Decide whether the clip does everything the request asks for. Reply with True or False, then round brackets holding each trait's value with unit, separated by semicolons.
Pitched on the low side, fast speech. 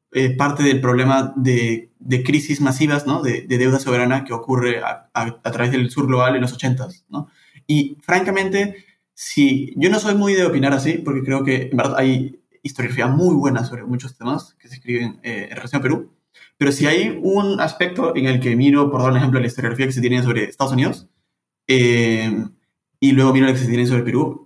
True (130 Hz; 215 wpm)